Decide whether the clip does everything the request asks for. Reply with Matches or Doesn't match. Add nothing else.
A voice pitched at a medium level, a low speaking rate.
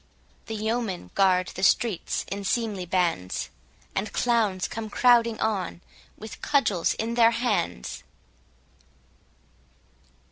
Doesn't match